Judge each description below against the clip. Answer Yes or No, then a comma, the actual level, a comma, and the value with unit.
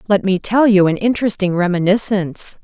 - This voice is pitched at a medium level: No, high, 195 Hz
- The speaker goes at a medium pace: Yes, average, 160 wpm